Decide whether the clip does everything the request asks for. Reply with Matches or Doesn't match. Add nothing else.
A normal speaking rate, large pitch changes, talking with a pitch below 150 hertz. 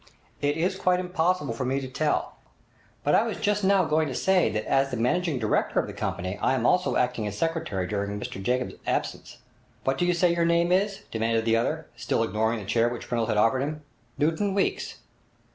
Doesn't match